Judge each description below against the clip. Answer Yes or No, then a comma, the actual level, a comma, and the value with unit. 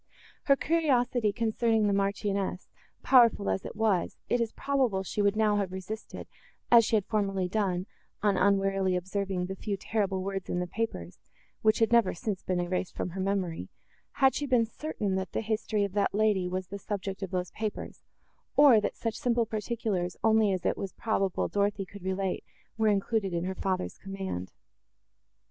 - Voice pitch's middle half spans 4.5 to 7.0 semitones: No, average, 2.8 semitones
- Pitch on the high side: Yes, high, 200 Hz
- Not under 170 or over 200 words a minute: Yes, average, 180 wpm